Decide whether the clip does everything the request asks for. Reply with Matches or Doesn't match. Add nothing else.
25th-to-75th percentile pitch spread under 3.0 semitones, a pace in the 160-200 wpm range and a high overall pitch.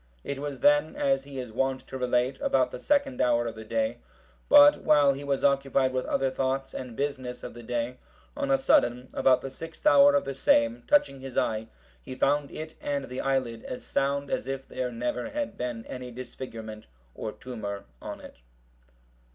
Doesn't match